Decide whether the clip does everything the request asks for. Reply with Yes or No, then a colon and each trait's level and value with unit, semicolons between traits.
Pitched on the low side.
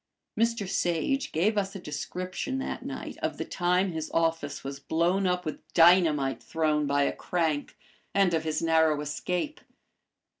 No: medium, 170 Hz